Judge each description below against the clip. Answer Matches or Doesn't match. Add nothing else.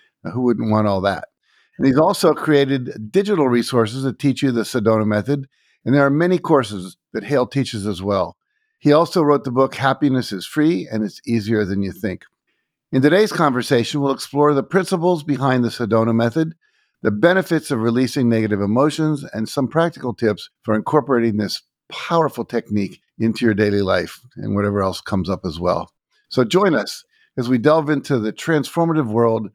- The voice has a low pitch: Matches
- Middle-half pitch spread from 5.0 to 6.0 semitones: Matches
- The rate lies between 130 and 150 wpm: Doesn't match